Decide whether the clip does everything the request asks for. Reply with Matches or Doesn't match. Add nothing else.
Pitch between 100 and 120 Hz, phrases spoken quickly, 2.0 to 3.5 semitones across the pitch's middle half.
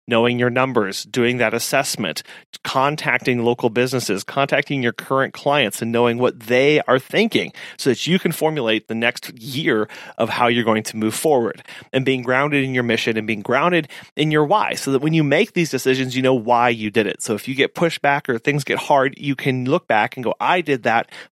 Doesn't match